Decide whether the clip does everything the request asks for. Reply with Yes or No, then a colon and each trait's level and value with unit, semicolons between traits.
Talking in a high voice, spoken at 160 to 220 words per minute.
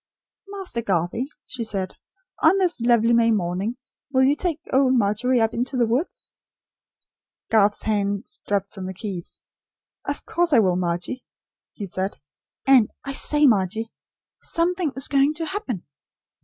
No: high, 235 Hz; average, 145 wpm